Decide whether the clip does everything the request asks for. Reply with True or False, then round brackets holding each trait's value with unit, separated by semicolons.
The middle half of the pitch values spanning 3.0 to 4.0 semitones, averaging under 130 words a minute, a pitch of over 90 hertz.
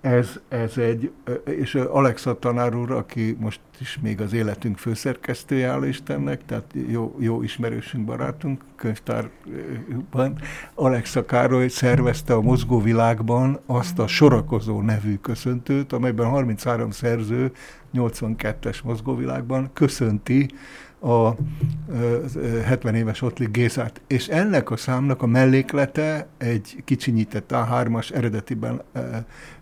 False (2.6 semitones; 105 wpm; 120 Hz)